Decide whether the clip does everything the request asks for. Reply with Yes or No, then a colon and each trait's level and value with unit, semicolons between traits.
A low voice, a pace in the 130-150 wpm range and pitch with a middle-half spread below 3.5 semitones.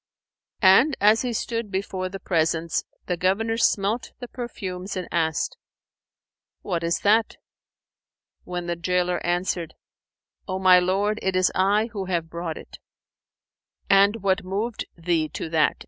No: medium, 185 Hz; average, 140 wpm; average, 2.9 semitones